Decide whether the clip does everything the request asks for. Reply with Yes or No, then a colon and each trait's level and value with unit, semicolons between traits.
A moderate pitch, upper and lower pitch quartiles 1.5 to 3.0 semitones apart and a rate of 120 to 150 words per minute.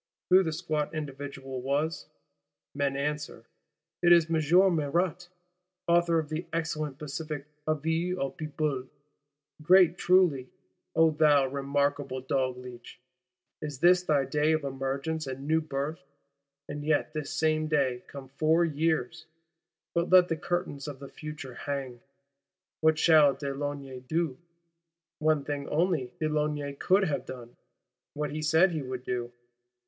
Yes: medium, 150 Hz; average, 2.7 semitones; slow, 135 wpm